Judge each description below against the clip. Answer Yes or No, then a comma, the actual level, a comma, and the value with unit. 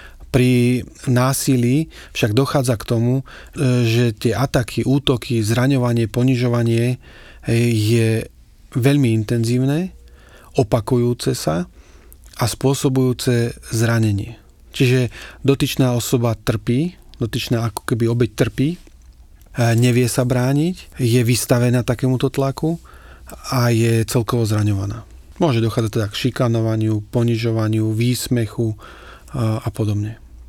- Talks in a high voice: No, low, 120 Hz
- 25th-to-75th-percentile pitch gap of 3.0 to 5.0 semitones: No, narrow, 2.4 semitones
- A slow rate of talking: Yes, slow, 95 wpm